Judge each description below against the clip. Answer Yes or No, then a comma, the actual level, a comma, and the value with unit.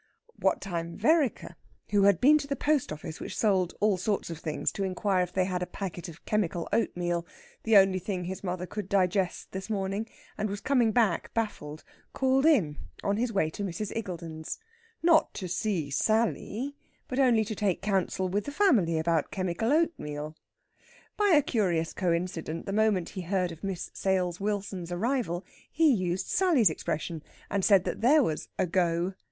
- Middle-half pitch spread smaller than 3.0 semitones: No, average, 4.2 semitones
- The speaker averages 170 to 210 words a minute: Yes, average, 180 wpm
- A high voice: Yes, high, 195 Hz